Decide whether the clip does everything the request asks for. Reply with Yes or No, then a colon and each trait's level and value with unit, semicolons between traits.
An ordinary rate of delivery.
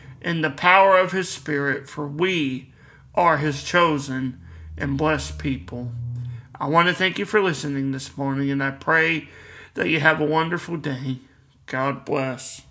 Yes: average, 160 wpm